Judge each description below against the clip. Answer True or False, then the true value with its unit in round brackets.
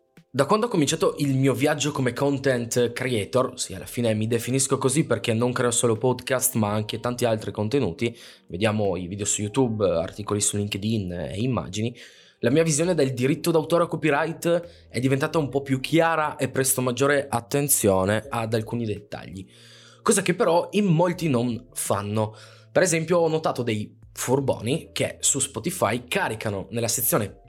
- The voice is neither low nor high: False (125 Hz)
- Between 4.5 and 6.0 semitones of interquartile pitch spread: True (5.2 semitones)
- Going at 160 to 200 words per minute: True (165 wpm)